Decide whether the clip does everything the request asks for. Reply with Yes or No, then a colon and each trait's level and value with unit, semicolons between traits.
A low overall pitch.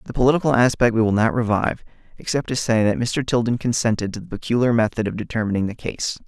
Yes: low, 115 Hz